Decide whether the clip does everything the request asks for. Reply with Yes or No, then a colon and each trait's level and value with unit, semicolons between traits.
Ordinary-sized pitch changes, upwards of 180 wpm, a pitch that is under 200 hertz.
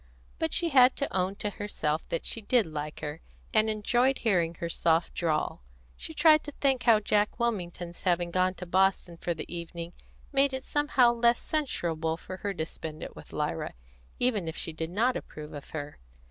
No: wide, 6.4 semitones; average, 190 wpm; medium, 185 Hz